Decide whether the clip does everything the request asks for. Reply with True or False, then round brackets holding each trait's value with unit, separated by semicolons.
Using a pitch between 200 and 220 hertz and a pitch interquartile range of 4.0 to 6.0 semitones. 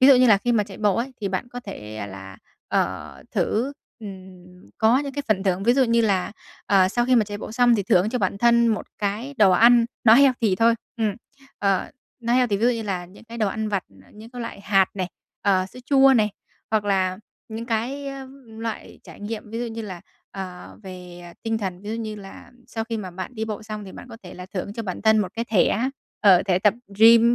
False (215 Hz; 3.4 semitones)